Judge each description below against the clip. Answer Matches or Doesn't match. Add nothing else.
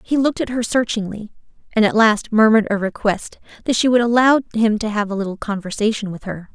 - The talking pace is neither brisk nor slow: Doesn't match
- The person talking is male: Doesn't match